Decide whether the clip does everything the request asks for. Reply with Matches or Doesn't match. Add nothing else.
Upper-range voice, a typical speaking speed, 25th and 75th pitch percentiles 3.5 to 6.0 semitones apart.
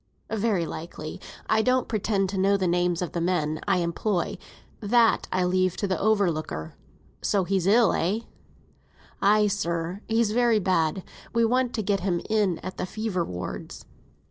Matches